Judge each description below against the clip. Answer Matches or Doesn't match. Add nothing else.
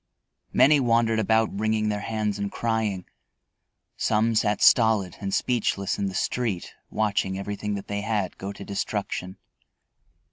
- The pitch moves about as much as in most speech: Doesn't match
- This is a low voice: Matches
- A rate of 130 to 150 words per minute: Matches